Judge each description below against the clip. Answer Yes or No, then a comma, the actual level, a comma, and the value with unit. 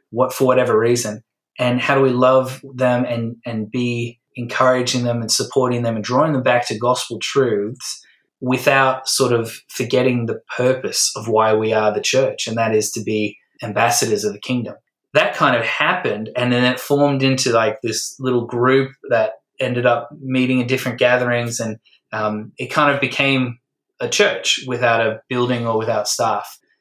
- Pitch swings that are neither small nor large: No, narrow, 2.1 semitones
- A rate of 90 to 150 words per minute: No, average, 180 wpm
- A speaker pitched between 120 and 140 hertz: Yes, low, 125 Hz